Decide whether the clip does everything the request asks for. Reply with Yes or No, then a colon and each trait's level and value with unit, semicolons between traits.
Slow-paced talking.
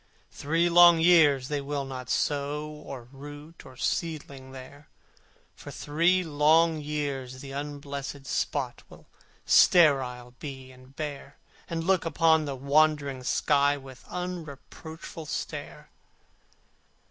Yes: slow, 120 wpm